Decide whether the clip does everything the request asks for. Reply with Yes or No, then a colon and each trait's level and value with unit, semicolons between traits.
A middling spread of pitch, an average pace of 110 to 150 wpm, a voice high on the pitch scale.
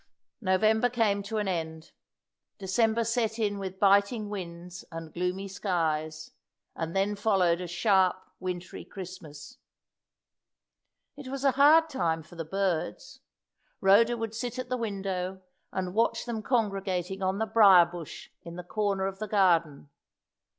Yes: average, 3.7 semitones; average, 145 wpm; high, 195 Hz